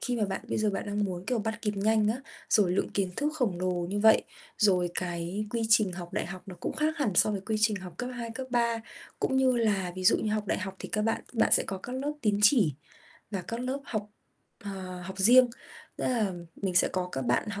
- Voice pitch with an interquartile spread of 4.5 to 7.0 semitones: No, average, 3.7 semitones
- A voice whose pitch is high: Yes, high, 210 Hz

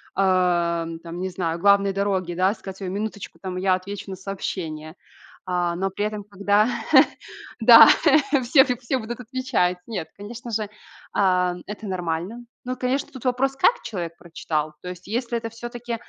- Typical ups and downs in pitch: Yes, average, 4.3 semitones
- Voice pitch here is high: Yes, high, 195 Hz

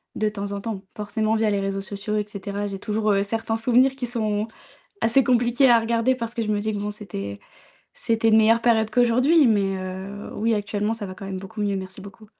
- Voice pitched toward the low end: No, high, 215 Hz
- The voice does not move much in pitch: Yes, narrow, 2.3 semitones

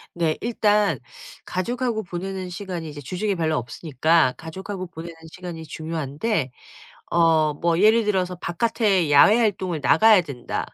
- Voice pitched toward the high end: No, medium, 175 Hz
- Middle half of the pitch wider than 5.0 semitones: No, average, 4.3 semitones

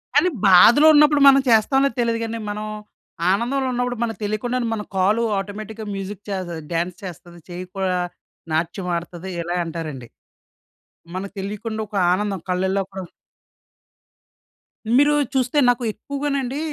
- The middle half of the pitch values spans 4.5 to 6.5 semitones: Yes, average, 5.0 semitones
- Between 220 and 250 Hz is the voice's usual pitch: No, high, 210 Hz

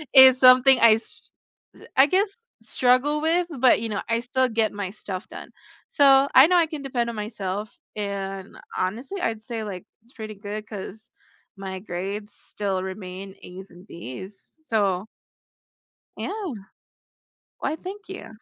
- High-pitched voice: Yes, high, 220 Hz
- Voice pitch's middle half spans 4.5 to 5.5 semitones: Yes, average, 5.1 semitones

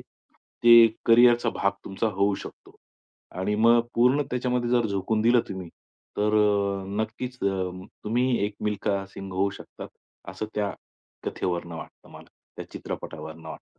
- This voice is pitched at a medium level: No, low, 105 Hz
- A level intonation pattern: No, average, 3.4 semitones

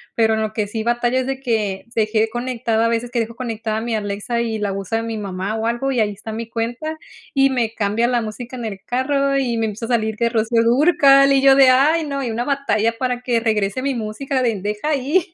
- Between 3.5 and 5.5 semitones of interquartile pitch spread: No, average, 2.9 semitones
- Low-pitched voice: No, high, 235 Hz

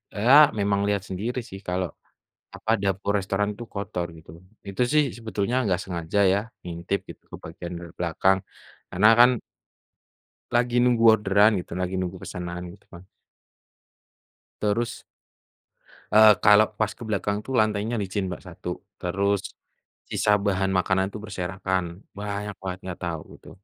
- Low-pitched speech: Yes, low, 100 Hz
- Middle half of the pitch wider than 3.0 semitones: No, narrow, 2.4 semitones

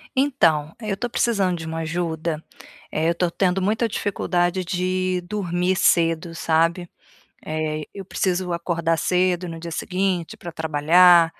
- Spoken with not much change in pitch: Yes, narrow, 2.0 semitones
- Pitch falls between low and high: Yes, medium, 175 Hz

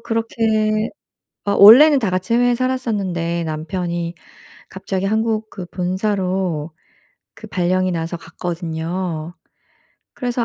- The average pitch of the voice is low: No, medium, 185 Hz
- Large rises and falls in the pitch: No, average, 4.2 semitones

